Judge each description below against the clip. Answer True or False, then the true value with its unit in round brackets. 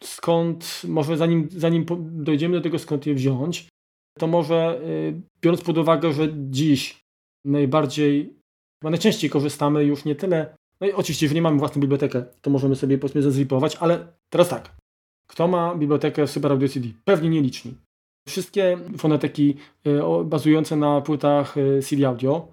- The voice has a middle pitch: True (150 Hz)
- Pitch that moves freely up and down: False (2.9 semitones)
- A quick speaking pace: False (150 wpm)